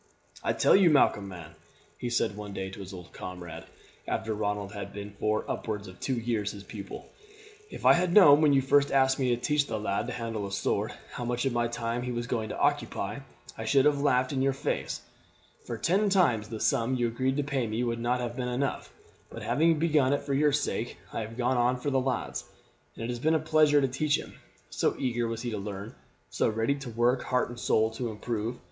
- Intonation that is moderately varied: Yes, average, 3.9 semitones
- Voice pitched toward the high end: No, low, 120 Hz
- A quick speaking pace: Yes, fast, 230 wpm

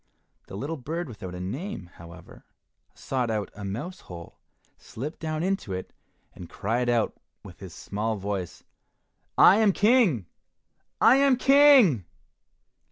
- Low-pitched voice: Yes, low, 125 Hz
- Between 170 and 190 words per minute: No, average, 145 wpm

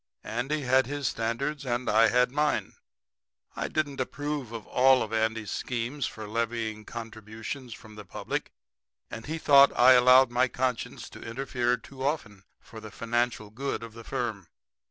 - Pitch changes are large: No, average, 3.0 semitones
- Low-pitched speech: Yes, low, 120 Hz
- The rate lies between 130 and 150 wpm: No, average, 160 wpm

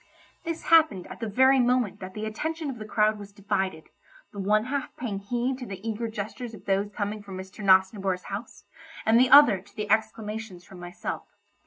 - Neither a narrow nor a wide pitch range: Yes, average, 3.7 semitones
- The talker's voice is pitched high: Yes, high, 215 Hz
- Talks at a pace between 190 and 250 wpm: Yes, average, 195 wpm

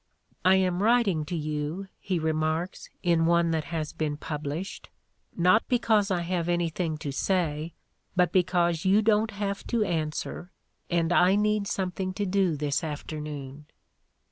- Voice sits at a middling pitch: Yes, medium, 175 Hz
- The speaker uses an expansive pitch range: No, average, 3.5 semitones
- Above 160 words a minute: No, average, 150 wpm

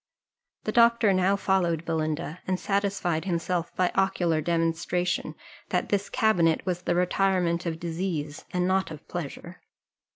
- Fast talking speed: No, slow, 135 wpm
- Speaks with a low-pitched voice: No, medium, 175 Hz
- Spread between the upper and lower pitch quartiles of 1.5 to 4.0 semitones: Yes, narrow, 2.6 semitones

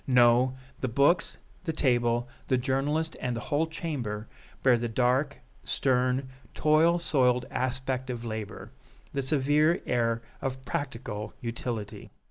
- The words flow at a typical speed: No, slow, 125 wpm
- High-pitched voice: No, low, 130 Hz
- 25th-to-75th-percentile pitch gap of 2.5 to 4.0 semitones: Yes, average, 3.2 semitones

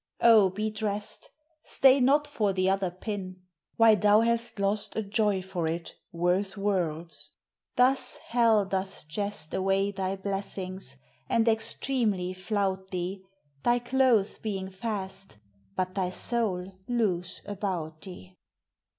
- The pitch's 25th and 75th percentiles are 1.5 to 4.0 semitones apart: Yes, average, 2.8 semitones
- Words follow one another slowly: Yes, slow, 125 wpm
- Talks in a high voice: Yes, high, 195 Hz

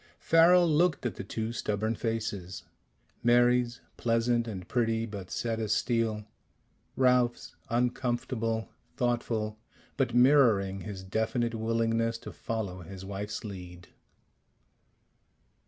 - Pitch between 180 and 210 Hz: No, low, 115 Hz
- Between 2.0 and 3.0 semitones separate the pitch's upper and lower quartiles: Yes, narrow, 2.6 semitones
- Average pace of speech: No, slow, 105 wpm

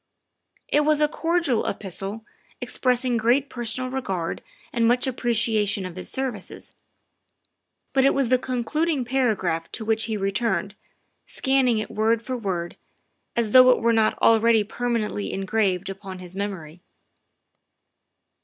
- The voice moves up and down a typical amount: Yes, average, 4.2 semitones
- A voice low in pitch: No, high, 230 Hz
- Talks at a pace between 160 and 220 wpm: No, average, 140 wpm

